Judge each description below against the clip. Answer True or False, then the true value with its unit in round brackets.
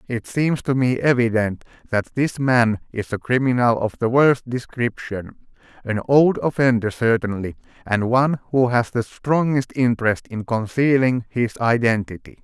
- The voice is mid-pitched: False (120 Hz)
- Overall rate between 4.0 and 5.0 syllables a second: True (4.5 syllables/s)